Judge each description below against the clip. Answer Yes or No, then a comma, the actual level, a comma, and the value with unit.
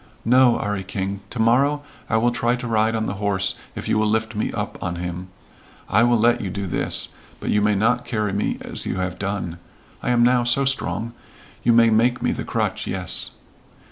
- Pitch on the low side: Yes, low, 110 Hz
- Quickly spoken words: Yes, fast, 210 wpm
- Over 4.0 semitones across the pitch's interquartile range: No, average, 3.4 semitones